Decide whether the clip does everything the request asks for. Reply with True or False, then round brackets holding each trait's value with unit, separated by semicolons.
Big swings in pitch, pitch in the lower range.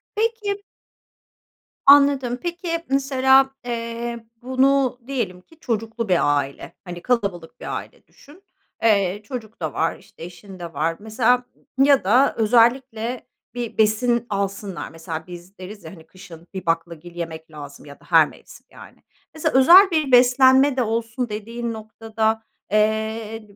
False (5.8 semitones; 225 Hz)